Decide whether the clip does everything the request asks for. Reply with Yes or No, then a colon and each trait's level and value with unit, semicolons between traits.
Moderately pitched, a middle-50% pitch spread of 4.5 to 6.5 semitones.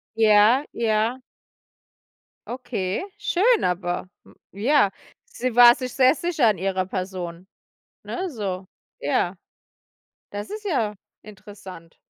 No: high, 215 Hz; average, 5.2 semitones